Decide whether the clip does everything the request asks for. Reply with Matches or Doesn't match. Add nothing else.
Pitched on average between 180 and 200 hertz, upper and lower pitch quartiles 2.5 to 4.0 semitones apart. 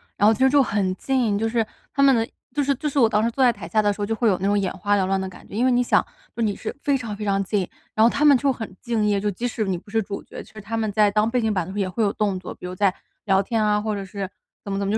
Doesn't match